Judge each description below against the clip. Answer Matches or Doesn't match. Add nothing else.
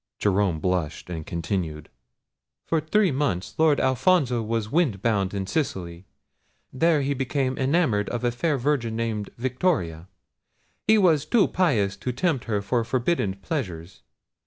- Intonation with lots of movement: Matches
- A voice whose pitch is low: Matches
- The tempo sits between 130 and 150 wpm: Matches